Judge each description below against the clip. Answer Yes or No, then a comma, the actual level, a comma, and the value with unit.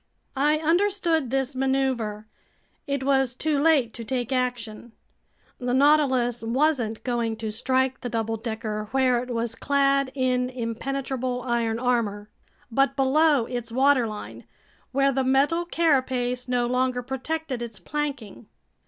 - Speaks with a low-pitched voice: No, very high, 255 Hz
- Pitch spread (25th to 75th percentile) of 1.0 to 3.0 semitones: Yes, narrow, 2.6 semitones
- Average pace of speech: No, slow, 130 wpm